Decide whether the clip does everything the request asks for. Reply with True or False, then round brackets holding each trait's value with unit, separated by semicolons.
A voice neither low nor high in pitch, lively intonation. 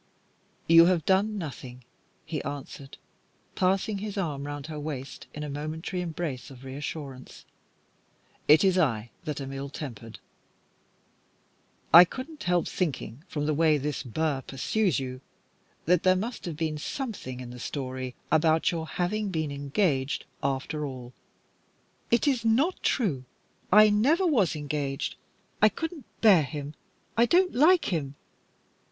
True (155 Hz; 5.9 semitones)